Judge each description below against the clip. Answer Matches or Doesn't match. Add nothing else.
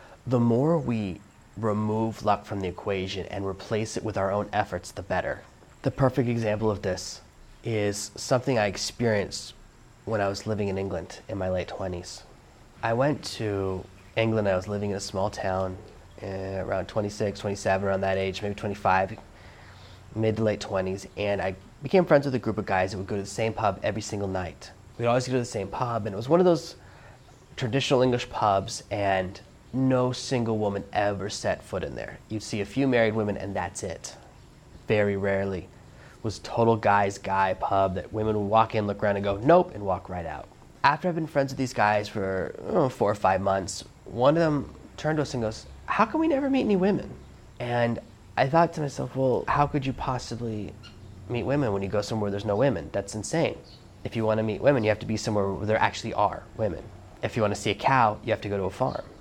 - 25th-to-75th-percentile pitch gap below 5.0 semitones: Matches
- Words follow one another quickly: Matches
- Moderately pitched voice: Doesn't match